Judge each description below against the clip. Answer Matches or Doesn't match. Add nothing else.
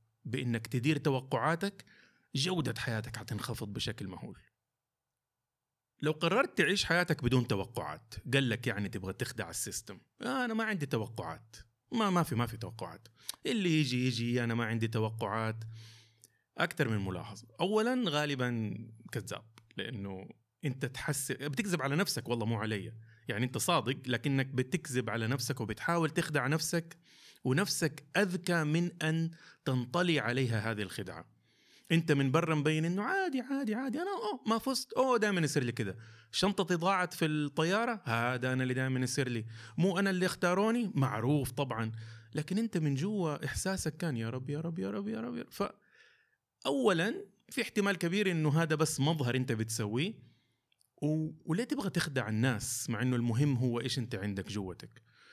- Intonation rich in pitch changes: Matches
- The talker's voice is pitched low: Matches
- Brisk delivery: Matches